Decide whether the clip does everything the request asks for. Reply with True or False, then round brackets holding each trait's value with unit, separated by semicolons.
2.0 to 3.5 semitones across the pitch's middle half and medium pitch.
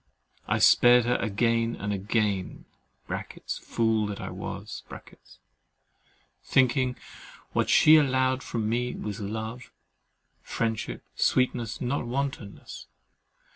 False (2.9 semitones; 115 Hz)